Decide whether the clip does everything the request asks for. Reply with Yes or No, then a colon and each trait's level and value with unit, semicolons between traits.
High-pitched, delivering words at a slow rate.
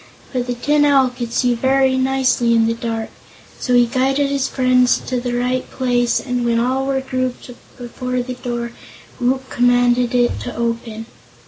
No: very high, 250 Hz; average, 175 wpm